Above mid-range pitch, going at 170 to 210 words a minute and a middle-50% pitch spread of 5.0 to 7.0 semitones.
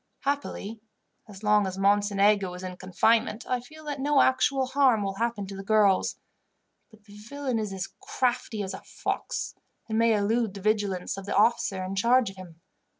No: high, 210 Hz; average, 185 wpm; average, 3.8 semitones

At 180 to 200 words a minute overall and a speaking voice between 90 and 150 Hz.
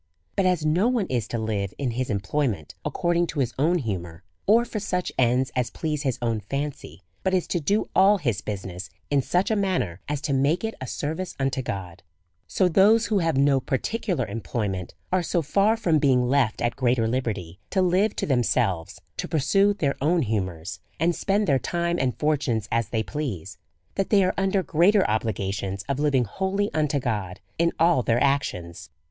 Yes: average, 195 wpm; medium, 140 Hz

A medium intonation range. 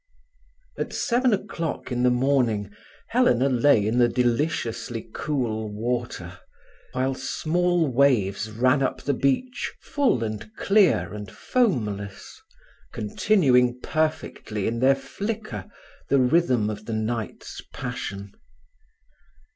No: wide, 5.7 semitones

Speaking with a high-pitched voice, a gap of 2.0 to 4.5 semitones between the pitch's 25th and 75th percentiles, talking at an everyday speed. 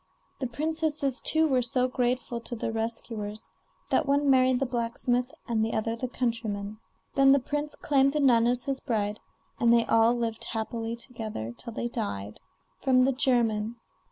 Yes: high, 240 Hz; average, 2.8 semitones; average, 170 wpm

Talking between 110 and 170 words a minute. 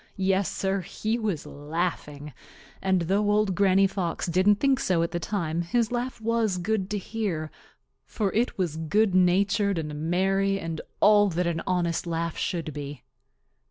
Yes: average, 160 wpm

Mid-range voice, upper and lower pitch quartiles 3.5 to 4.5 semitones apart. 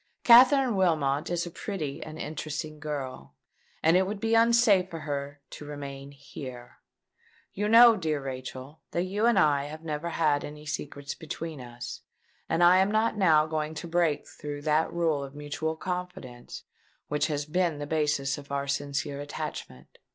Yes: medium, 155 Hz; average, 3.8 semitones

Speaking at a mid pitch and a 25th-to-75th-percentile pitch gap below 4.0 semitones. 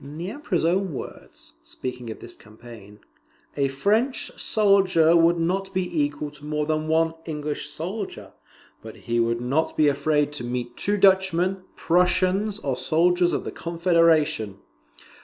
No: medium, 160 Hz; average, 4.4 semitones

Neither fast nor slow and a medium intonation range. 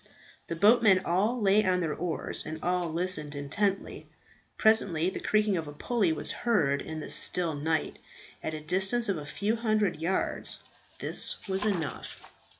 Yes: average, 160 wpm; average, 4.7 semitones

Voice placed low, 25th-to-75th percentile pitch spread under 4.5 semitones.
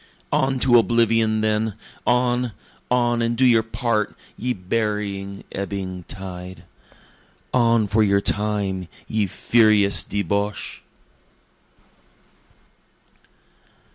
Yes: low, 105 Hz; average, 2.9 semitones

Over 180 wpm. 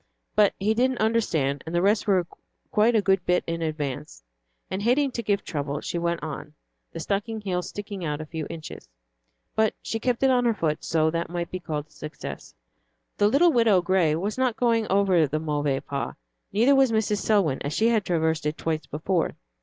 Yes: average, 200 wpm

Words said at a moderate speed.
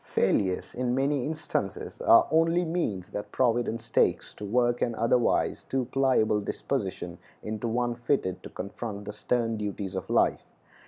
Yes: average, 150 wpm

